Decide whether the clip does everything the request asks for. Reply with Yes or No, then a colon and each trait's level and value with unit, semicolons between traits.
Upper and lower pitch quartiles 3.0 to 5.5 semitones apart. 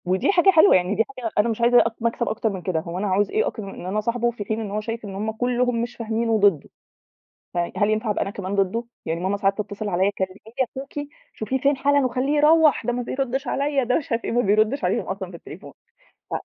Yes: average, 4.0 semitones